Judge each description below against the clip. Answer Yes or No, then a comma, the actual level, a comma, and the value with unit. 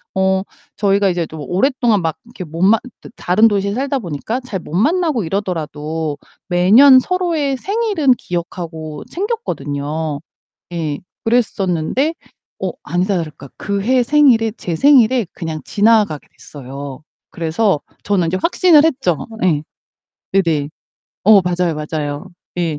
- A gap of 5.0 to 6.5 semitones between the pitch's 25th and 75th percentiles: No, wide, 7.5 semitones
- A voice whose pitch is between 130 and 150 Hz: No, high, 190 Hz